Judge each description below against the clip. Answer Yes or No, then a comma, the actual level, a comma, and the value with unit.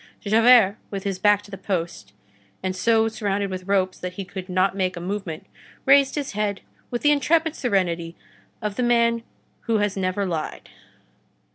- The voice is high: Yes, high, 200 Hz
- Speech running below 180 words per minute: Yes, average, 170 wpm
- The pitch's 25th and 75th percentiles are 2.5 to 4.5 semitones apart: Yes, average, 3.5 semitones